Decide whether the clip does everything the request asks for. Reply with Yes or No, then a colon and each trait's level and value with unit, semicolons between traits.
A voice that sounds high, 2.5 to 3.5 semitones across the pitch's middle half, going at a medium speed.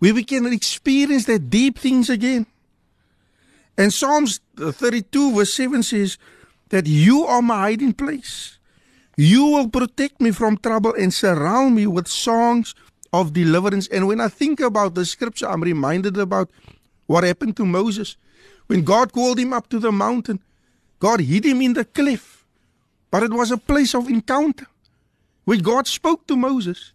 No: high, 235 Hz; average, 4.2 semitones; average, 165 wpm